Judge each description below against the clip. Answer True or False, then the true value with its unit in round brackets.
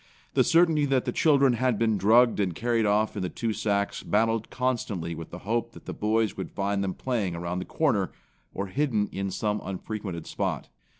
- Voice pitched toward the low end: True (105 Hz)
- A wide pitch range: False (3.6 semitones)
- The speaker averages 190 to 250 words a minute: True (195 wpm)